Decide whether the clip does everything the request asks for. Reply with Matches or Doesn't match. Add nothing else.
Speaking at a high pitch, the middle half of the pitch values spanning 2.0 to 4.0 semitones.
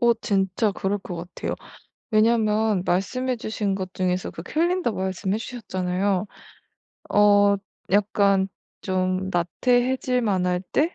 Matches